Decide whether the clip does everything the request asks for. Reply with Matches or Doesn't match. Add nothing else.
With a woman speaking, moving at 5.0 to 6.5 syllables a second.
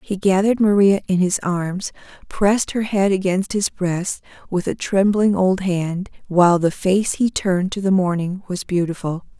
Doesn't match